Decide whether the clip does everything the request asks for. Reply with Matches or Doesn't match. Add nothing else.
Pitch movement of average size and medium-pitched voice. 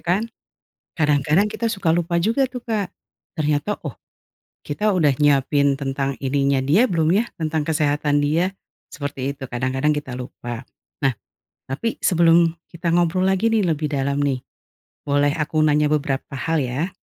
Matches